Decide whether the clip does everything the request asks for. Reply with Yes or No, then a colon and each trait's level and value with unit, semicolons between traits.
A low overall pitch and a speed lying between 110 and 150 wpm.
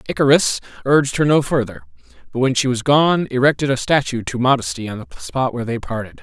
No: low, 130 Hz; fast, 205 wpm